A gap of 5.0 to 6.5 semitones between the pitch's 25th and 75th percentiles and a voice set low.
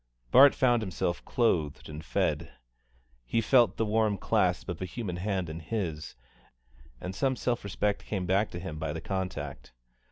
Yes: wide, 5.4 semitones; very low, 95 Hz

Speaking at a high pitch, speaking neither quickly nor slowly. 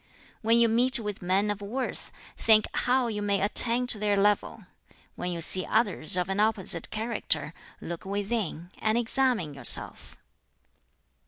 Yes: high, 210 Hz; average, 150 wpm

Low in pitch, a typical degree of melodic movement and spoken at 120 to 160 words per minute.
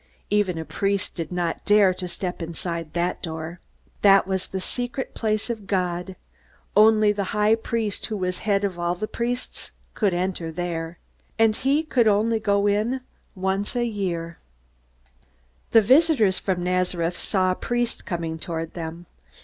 No: high, 190 Hz; average, 3.6 semitones; average, 155 wpm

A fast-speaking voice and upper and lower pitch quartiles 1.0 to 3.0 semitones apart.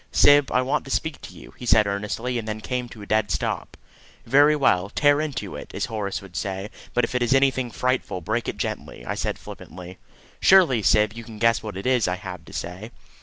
No: fast, 225 wpm; average, 4.2 semitones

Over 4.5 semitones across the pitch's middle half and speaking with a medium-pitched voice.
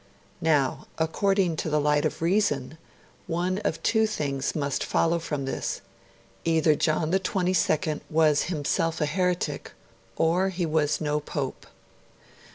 No: average, 3.2 semitones; medium, 160 Hz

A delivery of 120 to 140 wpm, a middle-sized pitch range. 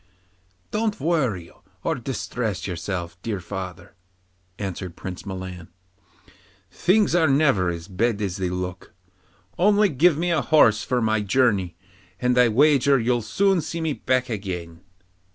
No: slow, 135 wpm; wide, 7.9 semitones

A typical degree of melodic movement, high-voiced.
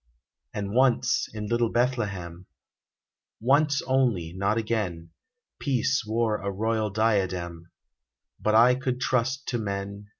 No: average, 4.2 semitones; low, 110 Hz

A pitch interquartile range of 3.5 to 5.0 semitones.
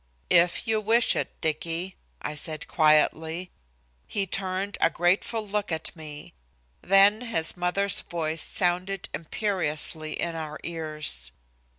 Yes: average, 3.8 semitones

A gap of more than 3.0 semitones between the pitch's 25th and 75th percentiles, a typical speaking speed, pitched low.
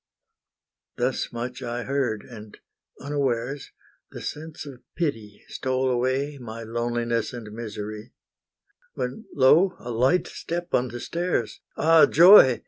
No: average, 3.5 semitones; slow, 125 wpm; low, 125 Hz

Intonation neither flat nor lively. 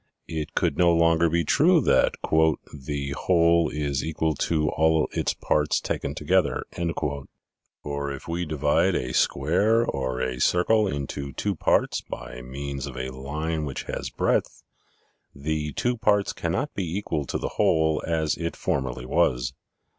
Yes: average, 3.3 semitones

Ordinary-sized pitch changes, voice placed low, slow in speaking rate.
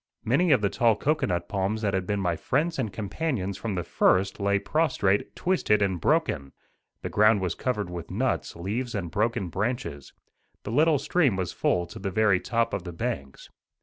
No: average, 4.8 semitones; low, 100 Hz; average, 185 wpm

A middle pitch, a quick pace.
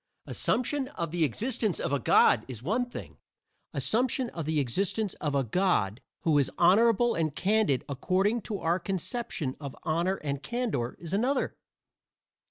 No: medium, 180 Hz; average, 155 wpm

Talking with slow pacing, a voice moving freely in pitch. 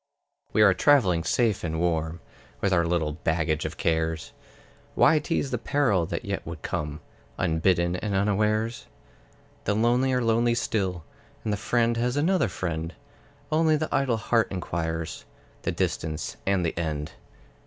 No: average, 150 wpm; wide, 6.3 semitones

